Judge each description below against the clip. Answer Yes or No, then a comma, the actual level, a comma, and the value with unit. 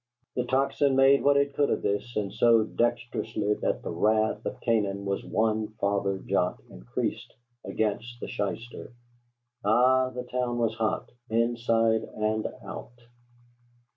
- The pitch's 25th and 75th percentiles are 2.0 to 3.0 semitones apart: Yes, narrow, 2.4 semitones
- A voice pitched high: No, low, 115 Hz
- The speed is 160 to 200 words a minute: No, average, 140 wpm